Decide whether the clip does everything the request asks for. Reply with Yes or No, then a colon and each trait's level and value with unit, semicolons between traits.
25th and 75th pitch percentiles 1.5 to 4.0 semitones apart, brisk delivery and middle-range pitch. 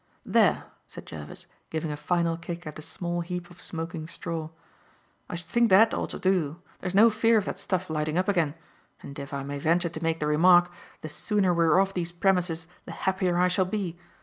Yes: narrow, 2.6 semitones; fast, 215 wpm; medium, 175 Hz